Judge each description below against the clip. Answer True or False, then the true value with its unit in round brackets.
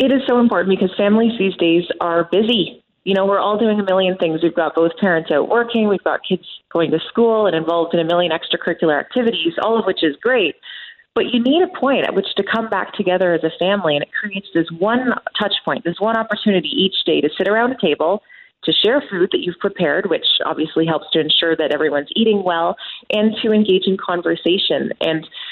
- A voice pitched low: False (195 Hz)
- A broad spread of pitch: False (4.9 semitones)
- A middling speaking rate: False (220 wpm)